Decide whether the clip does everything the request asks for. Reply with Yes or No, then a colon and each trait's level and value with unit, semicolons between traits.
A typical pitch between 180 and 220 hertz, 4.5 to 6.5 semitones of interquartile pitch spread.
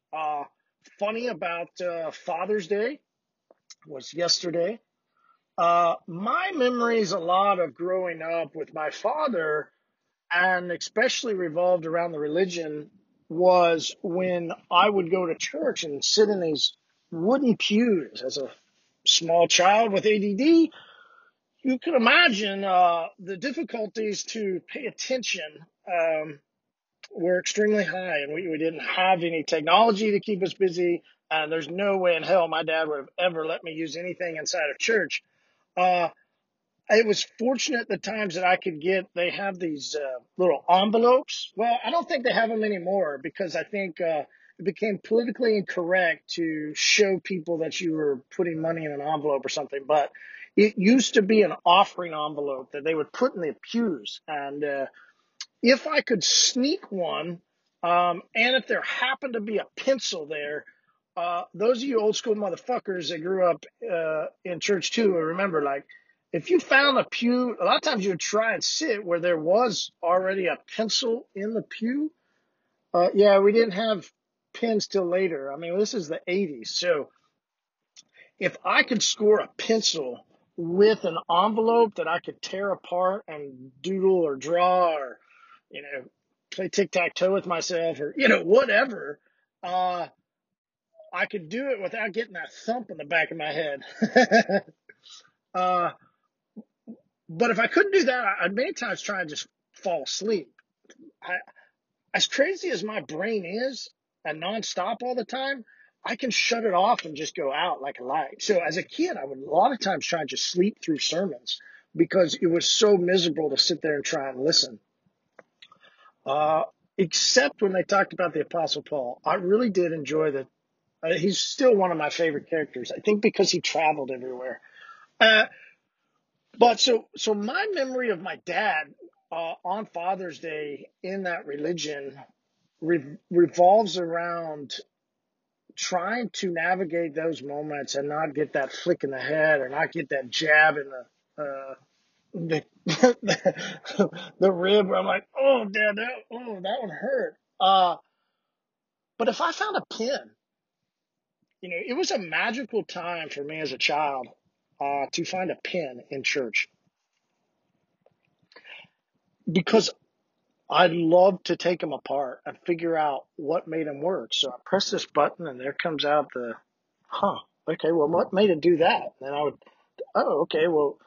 Yes: medium, 185 Hz; wide, 5.4 semitones